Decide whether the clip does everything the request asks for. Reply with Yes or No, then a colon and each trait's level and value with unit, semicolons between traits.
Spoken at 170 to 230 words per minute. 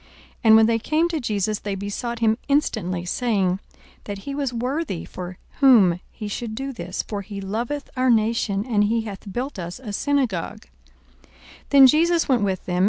Yes: average, 190 wpm